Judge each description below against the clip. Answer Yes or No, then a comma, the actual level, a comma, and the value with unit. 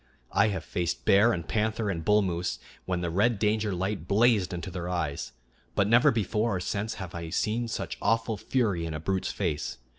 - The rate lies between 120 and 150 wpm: No, average, 200 wpm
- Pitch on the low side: Yes, low, 100 Hz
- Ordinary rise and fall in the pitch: Yes, average, 3.8 semitones